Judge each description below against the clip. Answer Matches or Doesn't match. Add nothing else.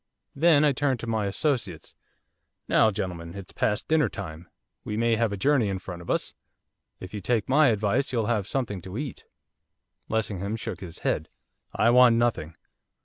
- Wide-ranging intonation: Doesn't match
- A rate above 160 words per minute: Matches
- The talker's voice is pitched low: Matches